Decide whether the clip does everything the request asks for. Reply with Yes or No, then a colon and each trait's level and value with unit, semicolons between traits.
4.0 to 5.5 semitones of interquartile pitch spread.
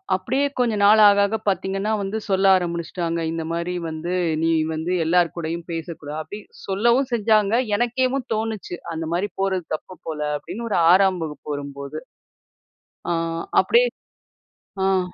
Yes: average, 4.4 semitones